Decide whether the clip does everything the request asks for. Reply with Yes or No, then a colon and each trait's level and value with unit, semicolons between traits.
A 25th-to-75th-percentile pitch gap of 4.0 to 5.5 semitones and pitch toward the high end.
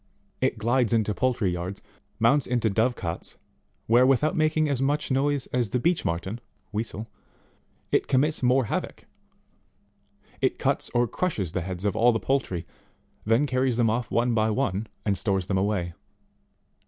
No: average, 4.3 semitones; low, 115 Hz